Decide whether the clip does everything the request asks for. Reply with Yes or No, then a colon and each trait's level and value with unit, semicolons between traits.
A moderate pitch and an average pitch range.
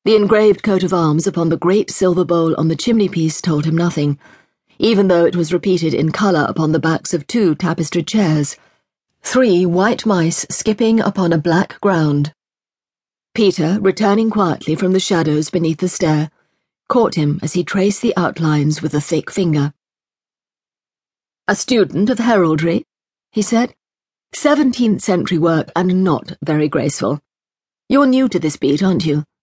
Yes: medium, 175 Hz; average, 4.1 semitones